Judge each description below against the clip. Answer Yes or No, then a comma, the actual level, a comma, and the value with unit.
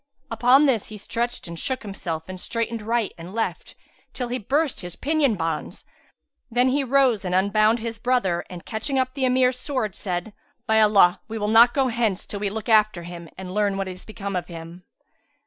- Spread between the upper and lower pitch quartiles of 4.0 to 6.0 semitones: Yes, average, 4.9 semitones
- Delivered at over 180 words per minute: Yes, average, 200 wpm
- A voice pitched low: No, high, 215 Hz